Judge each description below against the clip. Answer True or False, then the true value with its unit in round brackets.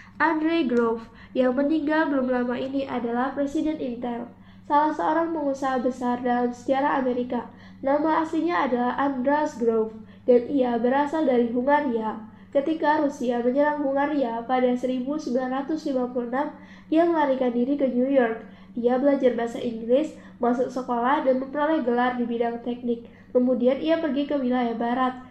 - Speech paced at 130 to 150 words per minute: True (135 wpm)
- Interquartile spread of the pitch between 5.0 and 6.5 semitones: False (2.9 semitones)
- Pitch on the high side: True (255 Hz)